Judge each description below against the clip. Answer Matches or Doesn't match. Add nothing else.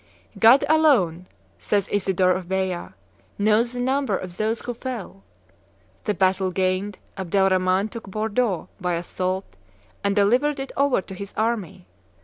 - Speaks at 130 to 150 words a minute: Matches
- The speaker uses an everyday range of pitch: Matches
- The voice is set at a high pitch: Matches